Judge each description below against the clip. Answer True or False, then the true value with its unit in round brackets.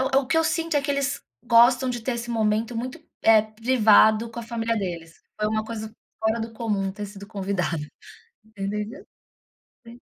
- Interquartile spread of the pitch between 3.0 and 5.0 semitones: False (2.5 semitones)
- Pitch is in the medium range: False (225 Hz)